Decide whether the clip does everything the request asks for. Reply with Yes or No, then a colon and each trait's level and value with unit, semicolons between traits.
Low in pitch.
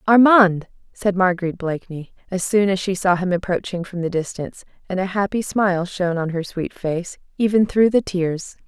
No: medium, 185 Hz